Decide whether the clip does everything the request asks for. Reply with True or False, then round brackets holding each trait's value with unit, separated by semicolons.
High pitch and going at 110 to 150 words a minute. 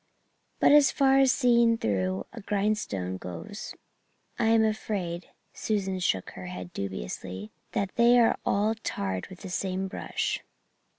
True (195 Hz; 145 wpm)